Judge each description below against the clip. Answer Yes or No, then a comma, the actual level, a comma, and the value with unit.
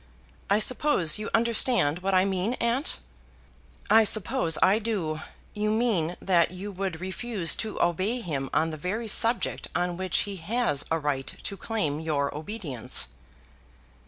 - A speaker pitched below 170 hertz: No, high, 190 Hz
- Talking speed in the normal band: Yes, average, 150 wpm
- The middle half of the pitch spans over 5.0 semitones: Yes, wide, 5.4 semitones